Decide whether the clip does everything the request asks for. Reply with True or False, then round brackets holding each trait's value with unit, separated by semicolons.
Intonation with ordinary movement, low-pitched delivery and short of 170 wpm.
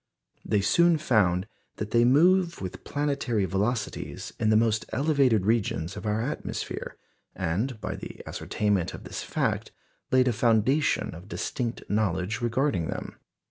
True (4.5 semitones; 110 Hz; 140 wpm)